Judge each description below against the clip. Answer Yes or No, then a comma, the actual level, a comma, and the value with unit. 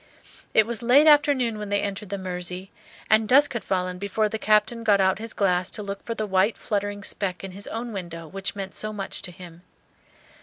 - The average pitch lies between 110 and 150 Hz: No, high, 205 Hz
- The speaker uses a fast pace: Yes, fast, 215 wpm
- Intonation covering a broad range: No, average, 2.8 semitones